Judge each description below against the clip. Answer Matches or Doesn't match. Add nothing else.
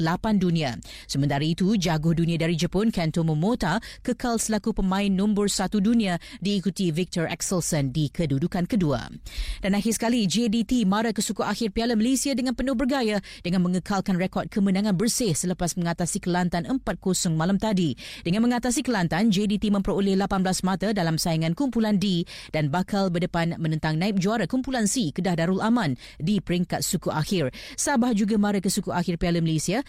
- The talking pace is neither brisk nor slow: Doesn't match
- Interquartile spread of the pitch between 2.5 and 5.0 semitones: Matches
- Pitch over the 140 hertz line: Matches